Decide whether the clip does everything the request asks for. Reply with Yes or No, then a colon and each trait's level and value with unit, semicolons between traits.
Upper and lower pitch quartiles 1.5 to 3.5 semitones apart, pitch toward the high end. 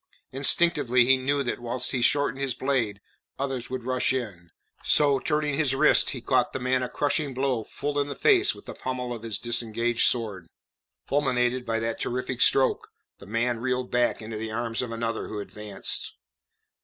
No: average, 2.8 semitones; low, 125 Hz